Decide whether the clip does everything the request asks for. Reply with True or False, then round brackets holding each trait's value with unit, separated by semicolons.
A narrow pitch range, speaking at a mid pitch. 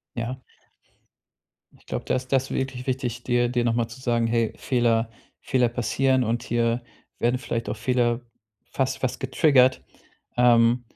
False (1.7 semitones; 120 Hz)